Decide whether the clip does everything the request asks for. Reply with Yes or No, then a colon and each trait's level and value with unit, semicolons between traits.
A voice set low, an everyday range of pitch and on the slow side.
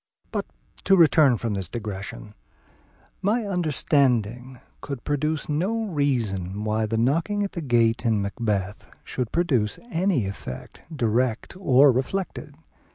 No: low, 130 Hz; wide, 6.6 semitones; slow, 125 wpm